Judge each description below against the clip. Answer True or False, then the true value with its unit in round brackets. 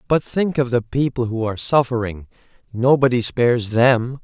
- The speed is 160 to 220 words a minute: False (140 wpm)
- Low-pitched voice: True (125 Hz)